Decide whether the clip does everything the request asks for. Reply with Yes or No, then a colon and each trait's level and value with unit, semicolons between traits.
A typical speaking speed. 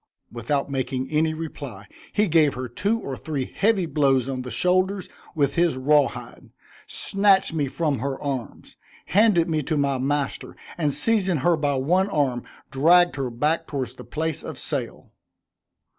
Yes: average, 160 wpm